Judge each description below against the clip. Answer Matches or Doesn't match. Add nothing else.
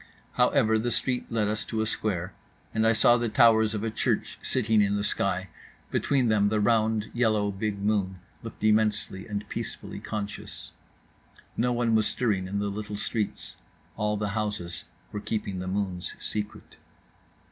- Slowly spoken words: Doesn't match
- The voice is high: Doesn't match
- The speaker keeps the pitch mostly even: Matches